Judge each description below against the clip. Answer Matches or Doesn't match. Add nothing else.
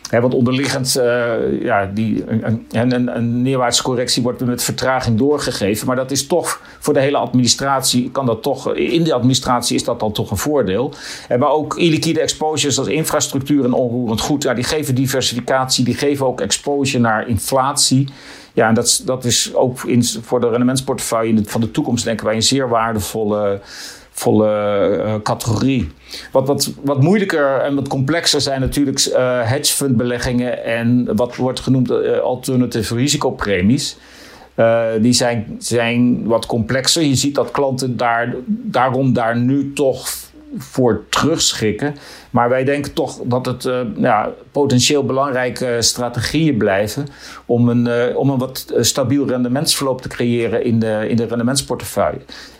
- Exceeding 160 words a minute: Doesn't match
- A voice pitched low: Matches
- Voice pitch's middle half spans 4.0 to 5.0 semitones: Doesn't match